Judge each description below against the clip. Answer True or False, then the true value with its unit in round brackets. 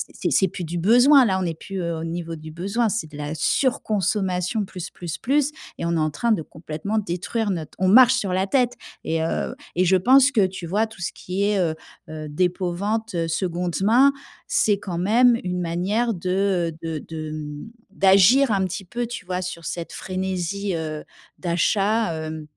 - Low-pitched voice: False (185 Hz)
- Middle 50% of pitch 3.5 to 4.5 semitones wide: True (4.2 semitones)